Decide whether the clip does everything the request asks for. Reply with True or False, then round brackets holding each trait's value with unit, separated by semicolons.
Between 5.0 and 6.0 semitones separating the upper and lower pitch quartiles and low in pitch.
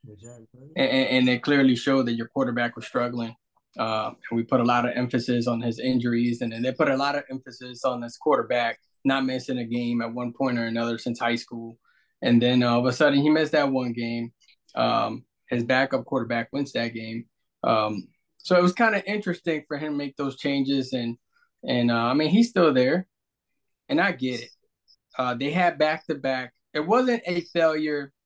False (3.8 semitones; 130 Hz)